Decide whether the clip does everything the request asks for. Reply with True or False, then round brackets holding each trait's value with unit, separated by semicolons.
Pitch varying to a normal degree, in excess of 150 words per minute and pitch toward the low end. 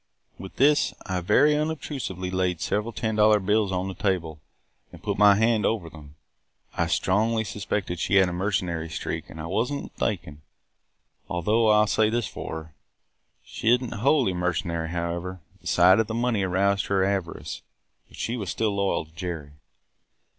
True (4.0 semitones; 180 wpm; 95 Hz)